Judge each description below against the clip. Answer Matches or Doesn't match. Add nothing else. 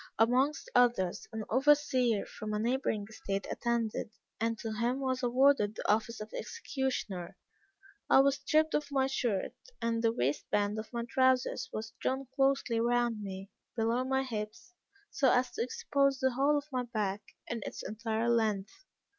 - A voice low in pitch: Doesn't match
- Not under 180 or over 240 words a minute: Doesn't match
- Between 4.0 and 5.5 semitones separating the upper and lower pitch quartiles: Doesn't match